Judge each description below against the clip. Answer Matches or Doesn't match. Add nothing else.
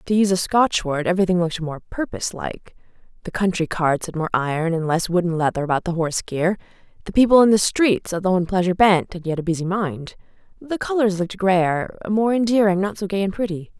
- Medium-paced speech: Doesn't match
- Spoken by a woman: Matches